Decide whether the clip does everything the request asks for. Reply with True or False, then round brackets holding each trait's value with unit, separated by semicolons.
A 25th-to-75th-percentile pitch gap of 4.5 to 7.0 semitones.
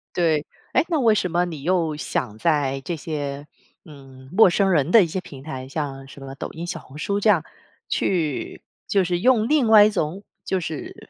True (5.3 semitones)